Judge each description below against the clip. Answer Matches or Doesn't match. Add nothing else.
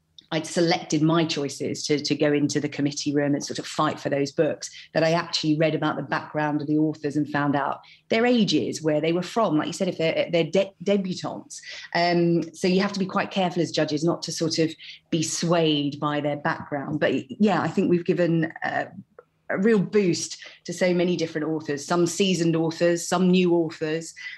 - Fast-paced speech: Matches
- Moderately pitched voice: Matches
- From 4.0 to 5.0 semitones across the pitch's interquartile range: Doesn't match